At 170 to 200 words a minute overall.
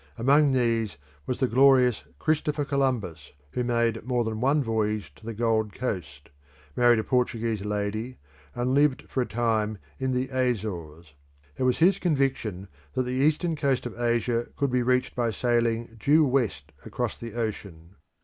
No: average, 160 wpm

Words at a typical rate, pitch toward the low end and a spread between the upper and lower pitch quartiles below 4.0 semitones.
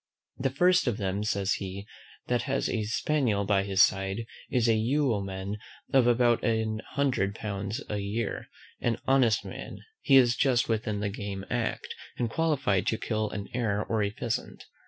Yes: average, 170 wpm; low, 110 Hz; average, 3.4 semitones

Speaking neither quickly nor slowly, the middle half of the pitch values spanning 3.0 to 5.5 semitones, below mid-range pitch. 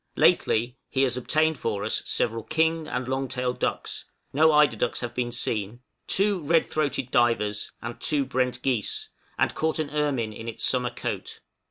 Yes: average, 175 wpm; average, 4.0 semitones; low, 125 Hz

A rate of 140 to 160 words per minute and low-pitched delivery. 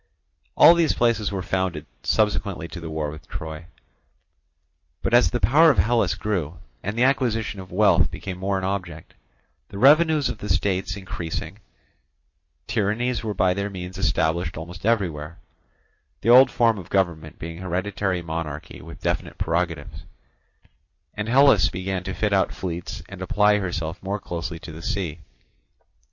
Yes: average, 150 wpm; very low, 95 Hz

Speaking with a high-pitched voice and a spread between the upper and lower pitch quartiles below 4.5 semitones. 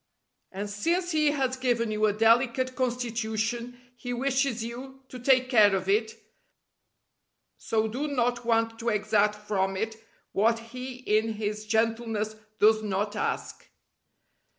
Yes: high, 230 Hz; average, 2.8 semitones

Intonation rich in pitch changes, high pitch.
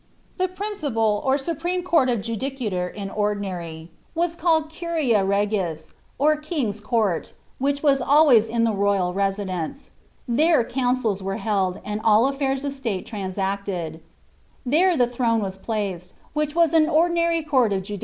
Yes: wide, 6.8 semitones; high, 230 Hz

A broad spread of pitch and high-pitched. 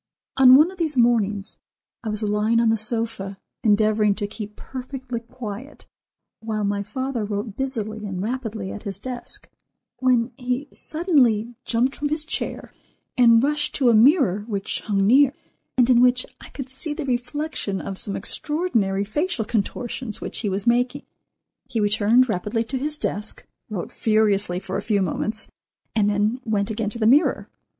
No: average, 3.8 semitones; high, 230 Hz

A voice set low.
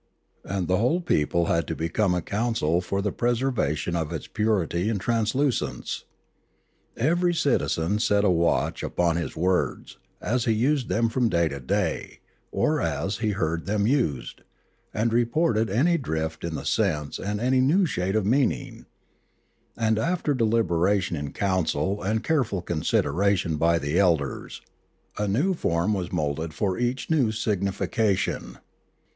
Yes: low, 100 Hz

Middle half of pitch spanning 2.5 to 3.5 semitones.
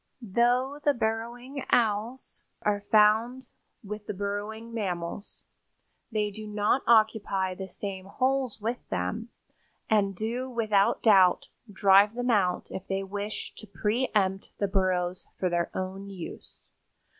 Yes: average, 3.1 semitones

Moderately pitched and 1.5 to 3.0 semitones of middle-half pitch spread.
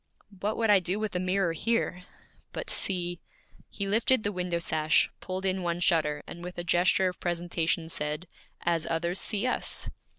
Yes: medium, 180 Hz; narrow, 2.4 semitones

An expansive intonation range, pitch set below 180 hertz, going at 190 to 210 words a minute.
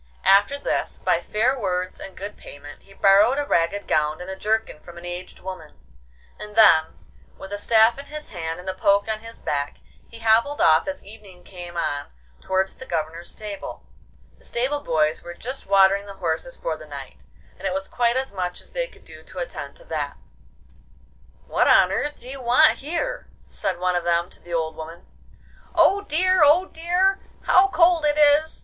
No: wide, 7.8 semitones; high, 200 Hz; average, 195 wpm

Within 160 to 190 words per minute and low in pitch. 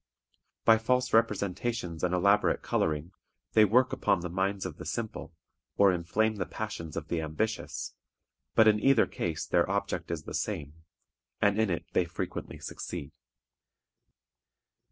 No: average, 145 wpm; low, 100 Hz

